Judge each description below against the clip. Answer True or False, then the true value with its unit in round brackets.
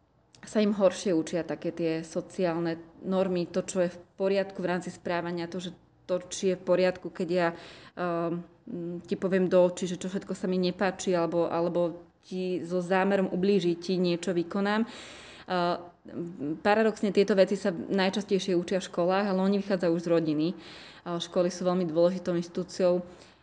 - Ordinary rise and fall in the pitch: False (1.8 semitones)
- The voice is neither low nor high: True (180 Hz)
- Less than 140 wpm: False (165 wpm)